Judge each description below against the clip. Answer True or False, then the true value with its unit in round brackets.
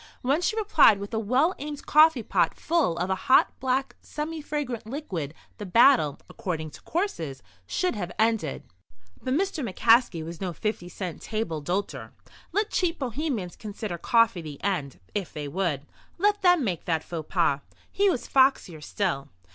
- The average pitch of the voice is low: False (215 Hz)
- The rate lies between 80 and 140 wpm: False (165 wpm)